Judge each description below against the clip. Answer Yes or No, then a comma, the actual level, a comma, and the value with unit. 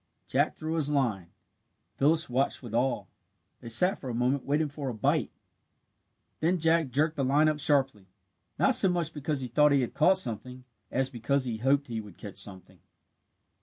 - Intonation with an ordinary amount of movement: Yes, average, 4.1 semitones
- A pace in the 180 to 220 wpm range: Yes, average, 185 wpm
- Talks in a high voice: No, low, 135 Hz